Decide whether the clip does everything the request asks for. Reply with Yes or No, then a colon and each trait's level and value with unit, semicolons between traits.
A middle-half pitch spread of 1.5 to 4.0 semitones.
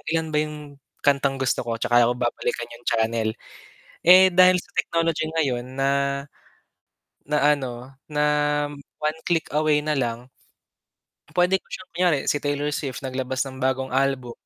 Yes: average, 3.3 semitones